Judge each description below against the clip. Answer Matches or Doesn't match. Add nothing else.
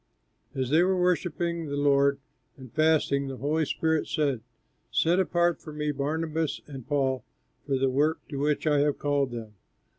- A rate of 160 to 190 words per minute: Matches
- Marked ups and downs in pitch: Doesn't match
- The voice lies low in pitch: Doesn't match